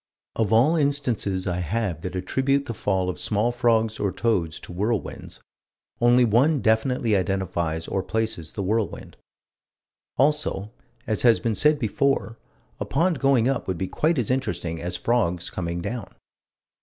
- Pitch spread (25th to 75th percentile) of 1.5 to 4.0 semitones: No, average, 5.1 semitones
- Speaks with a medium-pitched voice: No, low, 110 Hz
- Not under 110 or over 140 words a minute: No, average, 155 wpm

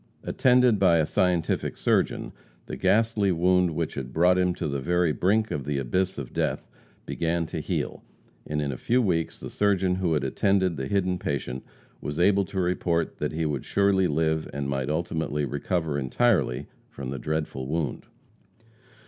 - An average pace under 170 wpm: No, average, 175 wpm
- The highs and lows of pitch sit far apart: No, average, 4.3 semitones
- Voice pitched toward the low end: Yes, very low, 85 Hz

